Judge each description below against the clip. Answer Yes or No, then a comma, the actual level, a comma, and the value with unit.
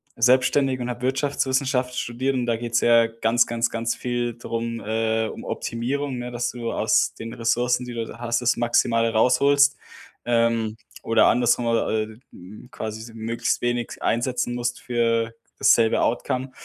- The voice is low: Yes, low, 120 Hz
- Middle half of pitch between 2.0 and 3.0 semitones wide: No, narrow, 1.3 semitones